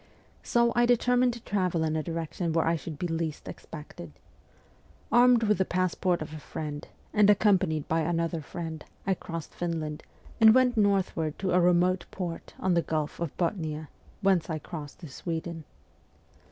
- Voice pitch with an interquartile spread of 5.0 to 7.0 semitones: No, average, 3.5 semitones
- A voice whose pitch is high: No, medium, 170 Hz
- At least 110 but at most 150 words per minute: No, average, 165 wpm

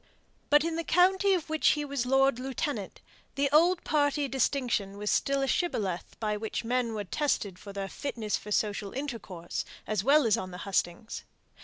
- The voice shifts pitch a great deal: Yes, wide, 6.0 semitones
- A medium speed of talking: Yes, average, 185 wpm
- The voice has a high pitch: Yes, very high, 255 Hz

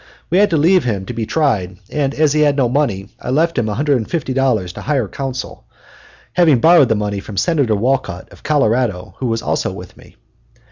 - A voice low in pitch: Yes, low, 130 Hz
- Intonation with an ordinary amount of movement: No, wide, 5.8 semitones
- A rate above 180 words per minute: Yes, average, 195 wpm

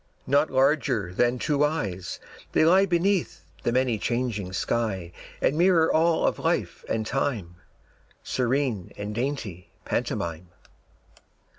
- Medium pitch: No, low, 125 Hz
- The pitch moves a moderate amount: No, wide, 6.7 semitones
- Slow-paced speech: Yes, slow, 120 wpm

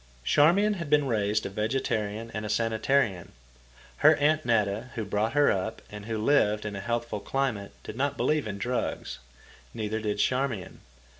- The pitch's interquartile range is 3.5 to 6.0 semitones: Yes, average, 4.5 semitones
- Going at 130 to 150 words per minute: No, average, 165 wpm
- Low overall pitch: Yes, low, 110 Hz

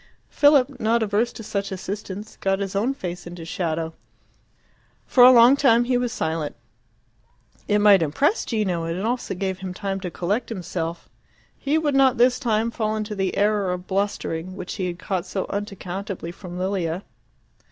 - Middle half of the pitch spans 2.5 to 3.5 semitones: No, average, 4.2 semitones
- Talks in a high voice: Yes, high, 200 Hz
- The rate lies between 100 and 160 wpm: No, average, 175 wpm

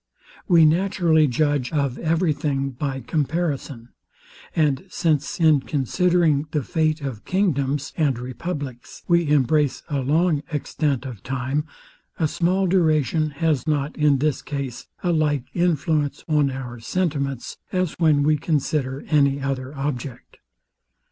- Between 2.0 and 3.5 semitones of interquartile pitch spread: Yes, average, 2.8 semitones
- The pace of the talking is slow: Yes, slow, 130 wpm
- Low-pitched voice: No, medium, 150 Hz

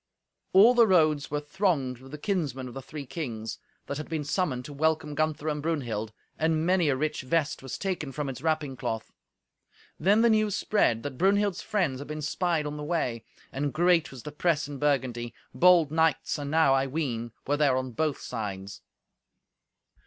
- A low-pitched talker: No, medium, 150 Hz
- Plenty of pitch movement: No, average, 3.8 semitones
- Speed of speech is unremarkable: Yes, average, 185 wpm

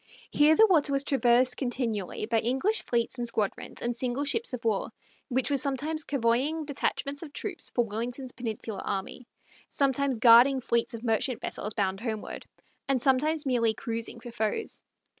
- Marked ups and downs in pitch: No, average, 3.4 semitones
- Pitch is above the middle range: Yes, very high, 250 Hz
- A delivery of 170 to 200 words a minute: No, average, 160 wpm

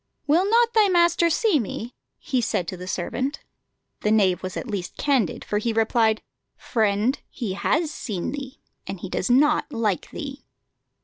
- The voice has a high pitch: Yes, high, 240 Hz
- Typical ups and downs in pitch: No, wide, 6.6 semitones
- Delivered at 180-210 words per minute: No, average, 170 wpm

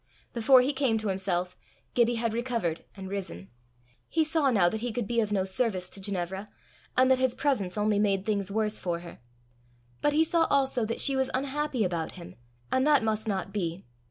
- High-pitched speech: Yes, high, 220 Hz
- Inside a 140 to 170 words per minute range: No, average, 200 wpm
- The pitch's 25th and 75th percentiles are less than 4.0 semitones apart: No, average, 5.2 semitones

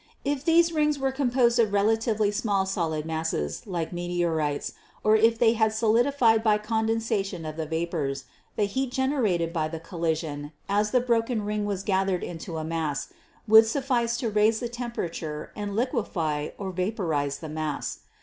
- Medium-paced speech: Yes, average, 160 wpm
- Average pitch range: No, wide, 6.0 semitones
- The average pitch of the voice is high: Yes, high, 205 Hz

